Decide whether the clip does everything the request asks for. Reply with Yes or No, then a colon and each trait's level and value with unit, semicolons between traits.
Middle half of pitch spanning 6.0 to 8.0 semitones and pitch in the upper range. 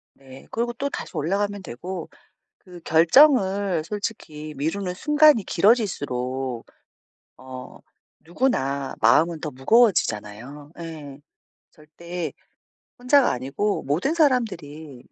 No: wide, 7.0 semitones; medium, 165 Hz